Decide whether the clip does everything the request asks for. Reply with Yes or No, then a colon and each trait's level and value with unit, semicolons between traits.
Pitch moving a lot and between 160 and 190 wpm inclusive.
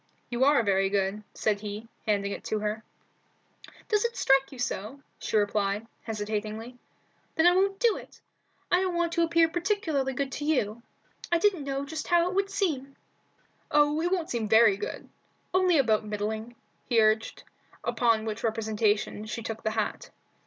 Yes: wide, 7.4 semitones; average, 170 wpm